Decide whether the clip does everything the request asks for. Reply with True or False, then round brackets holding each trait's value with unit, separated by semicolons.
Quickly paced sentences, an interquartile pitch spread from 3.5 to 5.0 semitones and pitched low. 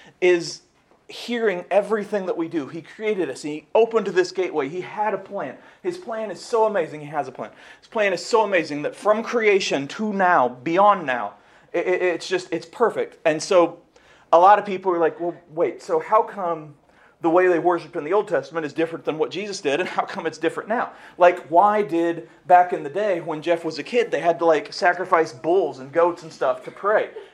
False (215 wpm; 4.1 semitones; 180 Hz)